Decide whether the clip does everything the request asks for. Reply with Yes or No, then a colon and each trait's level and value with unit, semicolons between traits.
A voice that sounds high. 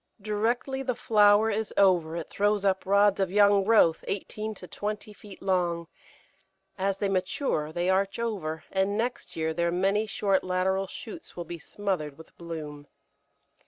Yes: high, 195 Hz